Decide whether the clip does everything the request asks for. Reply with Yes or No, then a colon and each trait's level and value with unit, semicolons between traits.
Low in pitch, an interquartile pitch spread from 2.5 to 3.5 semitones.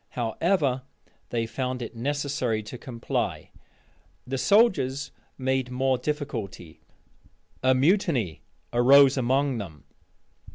Yes: low, 130 Hz; average, 2.9 semitones